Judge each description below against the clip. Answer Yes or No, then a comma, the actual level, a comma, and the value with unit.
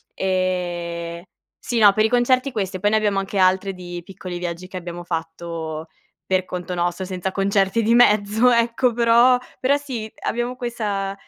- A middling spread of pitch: Yes, average, 4.6 semitones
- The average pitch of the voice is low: No, high, 195 Hz